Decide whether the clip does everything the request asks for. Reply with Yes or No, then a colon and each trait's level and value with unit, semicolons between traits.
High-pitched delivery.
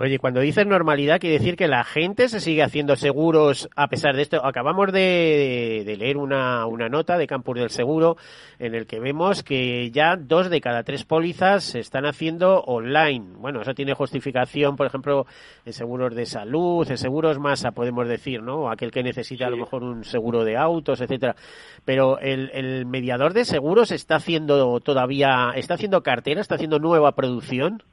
No: medium, 140 Hz